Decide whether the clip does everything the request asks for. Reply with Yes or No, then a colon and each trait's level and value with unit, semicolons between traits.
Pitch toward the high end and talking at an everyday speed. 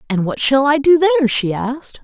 No: very high, 255 Hz; fast, 235 wpm